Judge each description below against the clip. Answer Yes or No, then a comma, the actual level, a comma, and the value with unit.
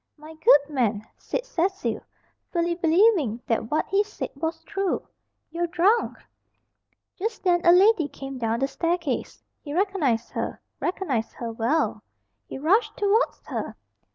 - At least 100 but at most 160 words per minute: Yes, average, 140 wpm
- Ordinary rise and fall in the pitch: No, wide, 6.1 semitones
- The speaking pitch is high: Yes, very high, 335 Hz